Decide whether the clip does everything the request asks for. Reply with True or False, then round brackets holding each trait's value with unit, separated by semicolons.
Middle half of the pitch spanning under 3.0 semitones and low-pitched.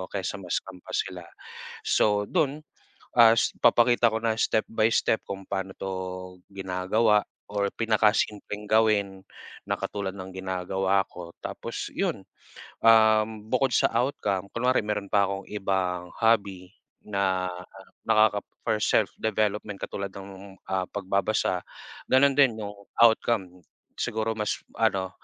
True (2.6 semitones; 105 Hz)